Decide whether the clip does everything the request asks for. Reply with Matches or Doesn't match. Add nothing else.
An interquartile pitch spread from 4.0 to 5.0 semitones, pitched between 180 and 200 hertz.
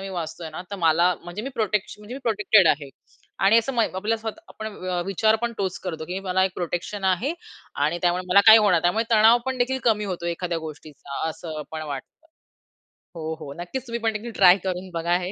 Matches